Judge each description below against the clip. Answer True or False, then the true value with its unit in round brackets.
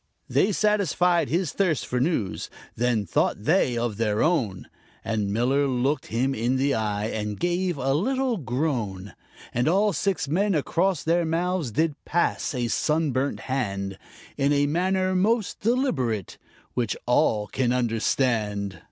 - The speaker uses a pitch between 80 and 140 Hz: True (135 Hz)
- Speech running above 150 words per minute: False (145 wpm)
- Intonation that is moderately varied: False (7.3 semitones)